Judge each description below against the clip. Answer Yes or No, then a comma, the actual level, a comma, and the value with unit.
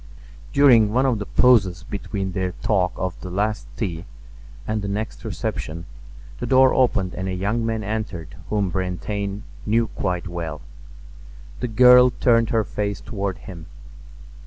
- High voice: No, low, 100 Hz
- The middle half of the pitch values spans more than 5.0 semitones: No, average, 3.5 semitones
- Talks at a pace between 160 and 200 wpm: No, average, 150 wpm